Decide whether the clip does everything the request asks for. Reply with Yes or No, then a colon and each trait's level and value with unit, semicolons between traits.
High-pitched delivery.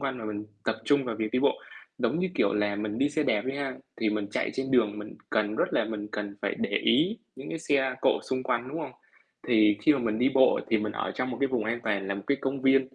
No: low, 120 Hz